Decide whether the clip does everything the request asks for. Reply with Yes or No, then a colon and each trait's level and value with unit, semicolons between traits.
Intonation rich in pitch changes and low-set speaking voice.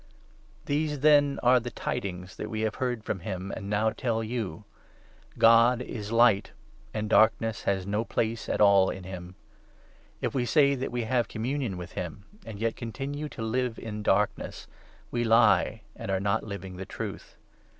No: average, 3.6 semitones; low, 110 Hz